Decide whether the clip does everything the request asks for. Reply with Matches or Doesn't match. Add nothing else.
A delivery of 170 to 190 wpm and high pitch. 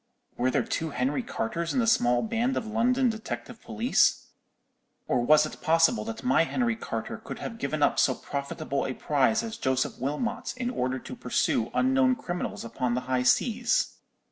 Doesn't match